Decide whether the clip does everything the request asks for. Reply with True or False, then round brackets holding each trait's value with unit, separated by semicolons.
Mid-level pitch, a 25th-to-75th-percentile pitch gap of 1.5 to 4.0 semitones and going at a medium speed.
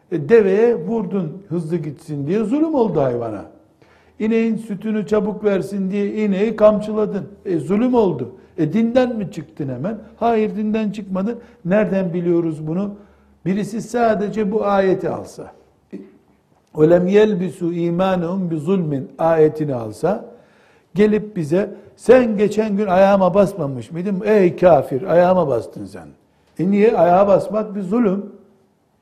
False (200 Hz; 3.5 semitones; 125 wpm)